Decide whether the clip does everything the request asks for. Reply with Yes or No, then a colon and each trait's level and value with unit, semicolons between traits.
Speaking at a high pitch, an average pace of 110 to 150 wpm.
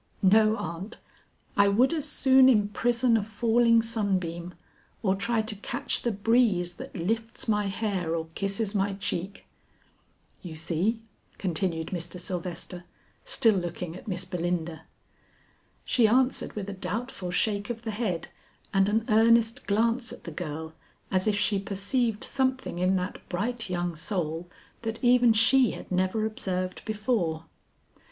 Yes: high, 205 Hz; average, 145 wpm